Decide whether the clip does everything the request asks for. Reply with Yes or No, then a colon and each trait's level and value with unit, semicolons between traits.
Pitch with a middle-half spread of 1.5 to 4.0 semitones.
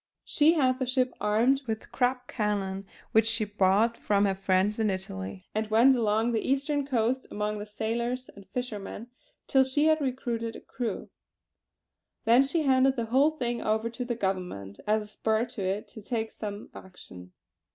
Yes: average, 3.6 semitones